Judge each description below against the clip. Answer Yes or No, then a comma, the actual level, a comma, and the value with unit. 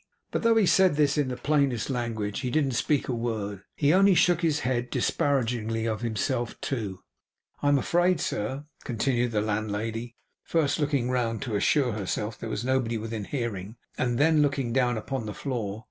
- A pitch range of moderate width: Yes, average, 4.3 semitones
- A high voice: No, low, 120 Hz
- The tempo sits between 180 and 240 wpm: Yes, average, 185 wpm